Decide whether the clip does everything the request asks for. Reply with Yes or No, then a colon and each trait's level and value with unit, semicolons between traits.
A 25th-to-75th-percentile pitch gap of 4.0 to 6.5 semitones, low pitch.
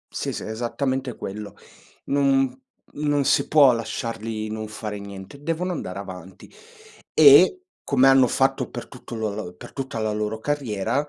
Yes: average, 4.7 semitones; low, 120 Hz